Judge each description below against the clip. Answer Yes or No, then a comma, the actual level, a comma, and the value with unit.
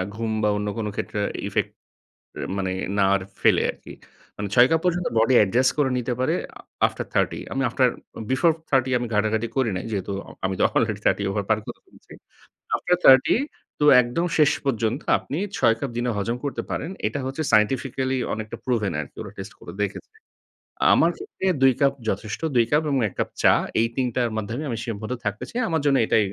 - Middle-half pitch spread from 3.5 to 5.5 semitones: Yes, average, 3.9 semitones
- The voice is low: Yes, low, 120 Hz